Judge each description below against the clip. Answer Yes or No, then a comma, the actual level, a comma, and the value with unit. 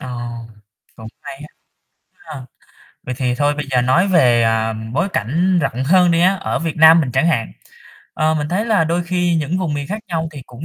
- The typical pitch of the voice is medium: Yes, medium, 155 Hz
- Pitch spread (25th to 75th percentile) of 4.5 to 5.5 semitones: Yes, average, 5.2 semitones